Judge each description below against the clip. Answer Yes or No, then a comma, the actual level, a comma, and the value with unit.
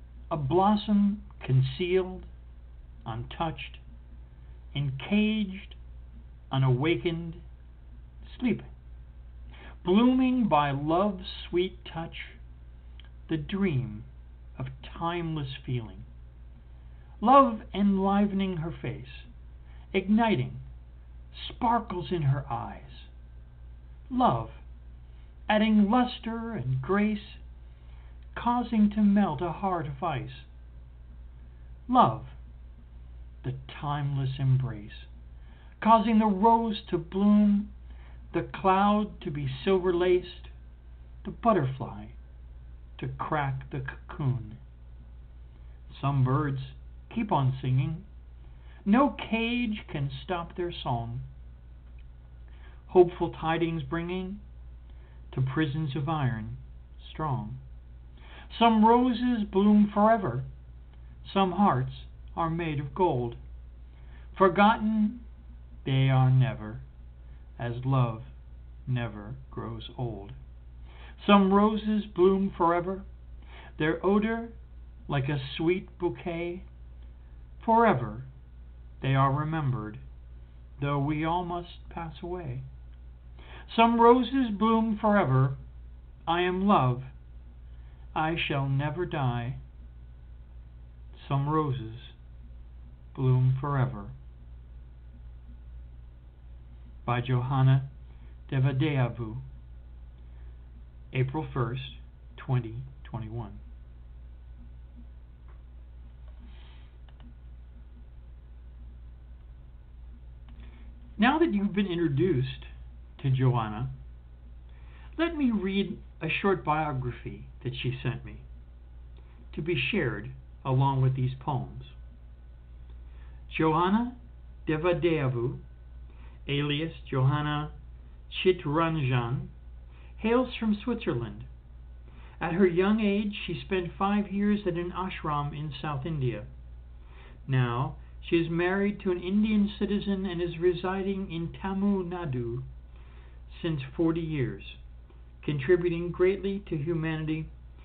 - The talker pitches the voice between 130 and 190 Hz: No, low, 120 Hz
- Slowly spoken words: Yes, slow, 85 wpm